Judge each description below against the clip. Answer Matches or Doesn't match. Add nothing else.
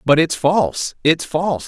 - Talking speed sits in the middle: Matches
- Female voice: Doesn't match